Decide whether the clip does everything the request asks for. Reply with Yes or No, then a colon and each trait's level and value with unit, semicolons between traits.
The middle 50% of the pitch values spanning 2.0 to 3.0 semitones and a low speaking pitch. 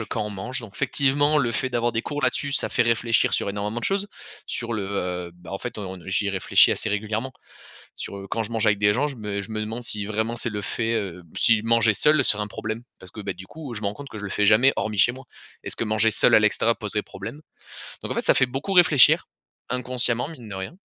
No: average, 3.4 semitones; low, 110 Hz